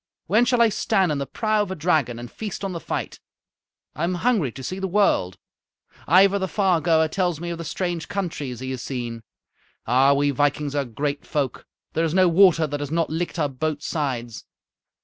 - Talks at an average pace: No, fast, 210 wpm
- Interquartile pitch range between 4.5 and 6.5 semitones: Yes, average, 4.9 semitones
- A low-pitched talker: No, medium, 160 Hz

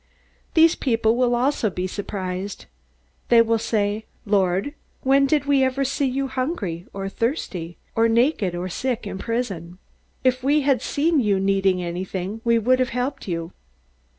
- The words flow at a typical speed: Yes, average, 160 wpm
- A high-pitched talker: Yes, high, 230 Hz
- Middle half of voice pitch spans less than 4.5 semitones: No, wide, 5.4 semitones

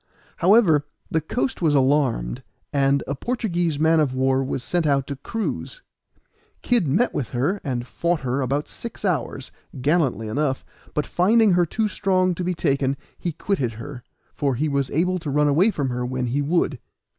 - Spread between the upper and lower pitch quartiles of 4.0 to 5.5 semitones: Yes, average, 4.9 semitones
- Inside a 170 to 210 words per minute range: Yes, average, 180 wpm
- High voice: No, medium, 145 Hz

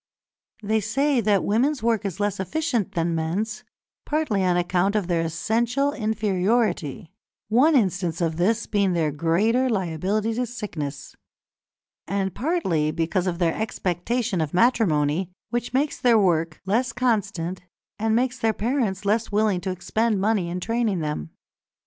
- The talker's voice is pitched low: No, high, 205 Hz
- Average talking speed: Yes, average, 145 wpm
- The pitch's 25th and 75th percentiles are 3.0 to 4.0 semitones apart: No, average, 4.9 semitones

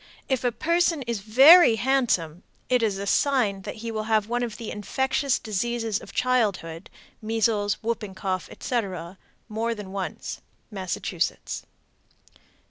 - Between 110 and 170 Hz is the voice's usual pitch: No, high, 225 Hz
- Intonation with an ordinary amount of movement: Yes, average, 3.6 semitones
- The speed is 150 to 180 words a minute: No, slow, 135 wpm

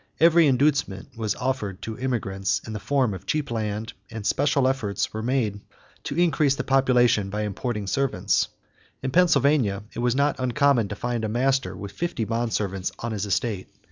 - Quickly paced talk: No, average, 175 wpm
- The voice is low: Yes, low, 120 Hz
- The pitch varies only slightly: No, average, 4.7 semitones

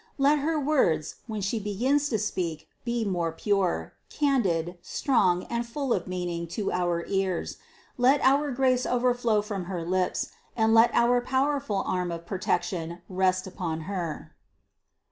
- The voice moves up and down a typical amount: No, wide, 5.8 semitones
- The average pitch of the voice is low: No, high, 200 Hz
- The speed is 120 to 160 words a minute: Yes, average, 145 wpm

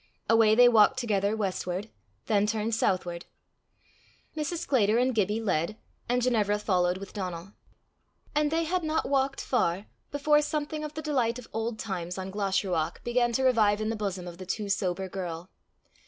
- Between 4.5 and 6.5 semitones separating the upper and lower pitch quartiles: Yes, average, 4.8 semitones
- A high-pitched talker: Yes, high, 215 Hz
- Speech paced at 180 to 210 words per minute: No, average, 170 wpm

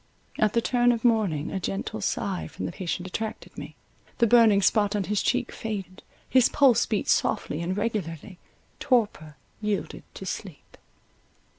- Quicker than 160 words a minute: No, average, 145 wpm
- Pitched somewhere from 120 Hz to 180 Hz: No, high, 210 Hz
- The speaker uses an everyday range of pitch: Yes, average, 3.6 semitones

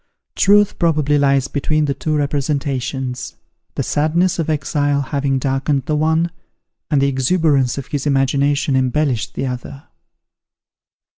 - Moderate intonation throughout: No, narrow, 2.2 semitones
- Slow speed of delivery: Yes, slow, 130 wpm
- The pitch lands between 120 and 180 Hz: Yes, medium, 140 Hz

